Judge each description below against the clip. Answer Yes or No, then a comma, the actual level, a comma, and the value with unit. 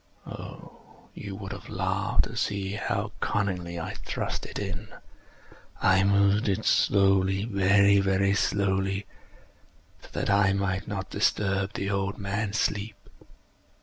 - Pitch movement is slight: Yes, narrow, 0.8 semitones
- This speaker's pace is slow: Yes, slow, 125 wpm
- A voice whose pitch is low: Yes, low, 100 Hz